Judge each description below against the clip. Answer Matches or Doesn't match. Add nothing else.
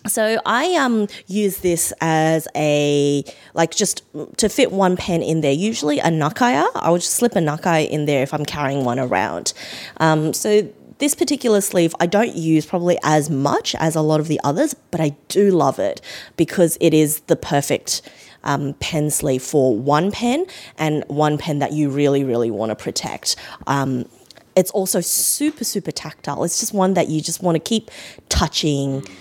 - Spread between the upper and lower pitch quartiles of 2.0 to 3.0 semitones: Doesn't match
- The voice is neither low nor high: Matches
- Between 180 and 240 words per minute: Matches